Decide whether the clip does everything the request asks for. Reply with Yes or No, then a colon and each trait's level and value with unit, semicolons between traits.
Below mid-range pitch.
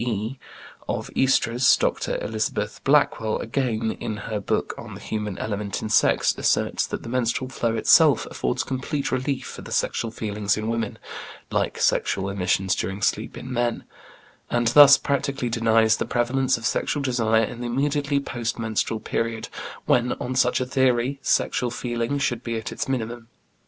Yes: low, 120 Hz